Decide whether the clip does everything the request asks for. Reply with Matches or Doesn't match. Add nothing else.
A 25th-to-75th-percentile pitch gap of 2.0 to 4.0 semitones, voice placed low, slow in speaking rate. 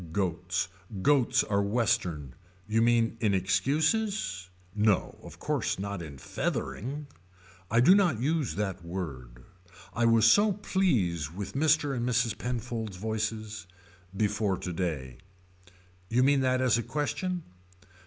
Doesn't match